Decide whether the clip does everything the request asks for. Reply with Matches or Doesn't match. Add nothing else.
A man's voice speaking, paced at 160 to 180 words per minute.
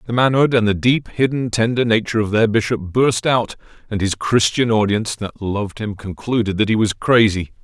Doesn't match